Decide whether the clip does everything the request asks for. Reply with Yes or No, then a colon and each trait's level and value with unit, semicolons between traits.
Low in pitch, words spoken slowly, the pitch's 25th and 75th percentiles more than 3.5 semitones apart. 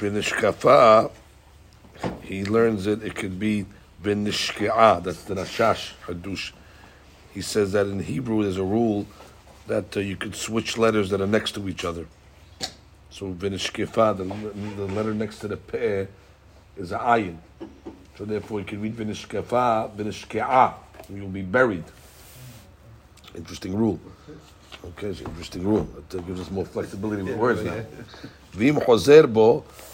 No: low, 100 Hz; slow, 130 wpm; average, 2.7 semitones